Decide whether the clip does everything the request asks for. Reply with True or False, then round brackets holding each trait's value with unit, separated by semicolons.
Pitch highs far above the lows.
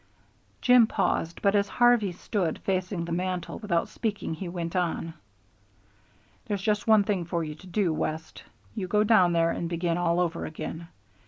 False (3.4 semitones)